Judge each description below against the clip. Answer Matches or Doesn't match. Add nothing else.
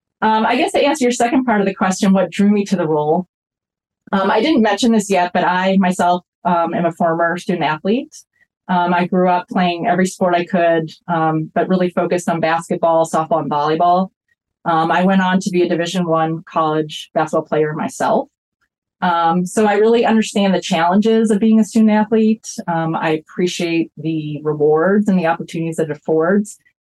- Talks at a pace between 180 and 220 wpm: Matches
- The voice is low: Doesn't match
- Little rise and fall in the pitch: Doesn't match